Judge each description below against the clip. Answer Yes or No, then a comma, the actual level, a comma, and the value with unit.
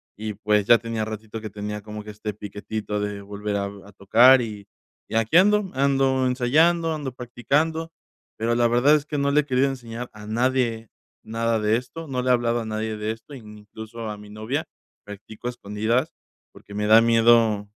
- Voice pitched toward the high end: No, low, 115 Hz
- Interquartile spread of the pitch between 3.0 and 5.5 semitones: Yes, average, 3.3 semitones